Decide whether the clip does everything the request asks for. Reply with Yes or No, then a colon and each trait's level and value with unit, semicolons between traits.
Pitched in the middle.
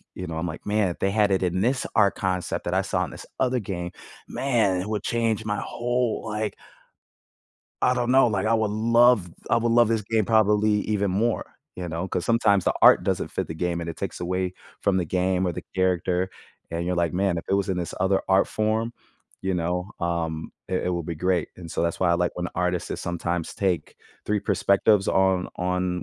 No: very low, 95 Hz